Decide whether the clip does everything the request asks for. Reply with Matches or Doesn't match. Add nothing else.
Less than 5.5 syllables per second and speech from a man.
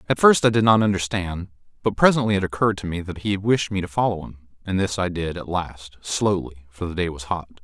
Doesn't match